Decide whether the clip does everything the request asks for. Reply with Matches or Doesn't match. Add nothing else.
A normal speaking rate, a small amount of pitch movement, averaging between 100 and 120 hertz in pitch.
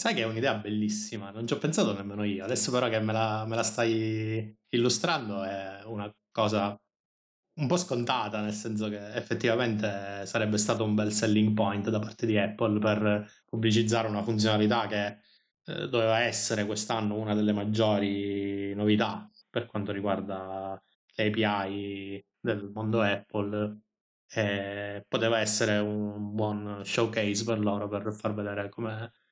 Matches